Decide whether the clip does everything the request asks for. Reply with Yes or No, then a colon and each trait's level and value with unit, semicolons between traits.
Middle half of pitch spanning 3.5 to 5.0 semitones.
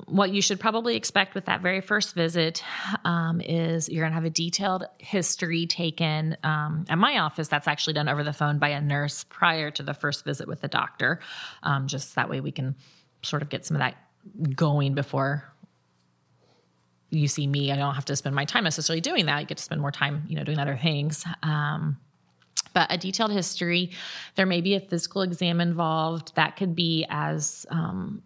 No: average, 3.1 semitones